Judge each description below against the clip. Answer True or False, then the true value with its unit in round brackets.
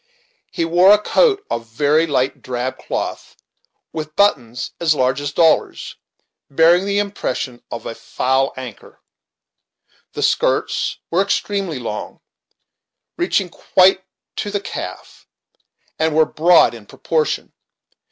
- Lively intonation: True (6.5 semitones)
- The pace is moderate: False (125 wpm)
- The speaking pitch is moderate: True (160 Hz)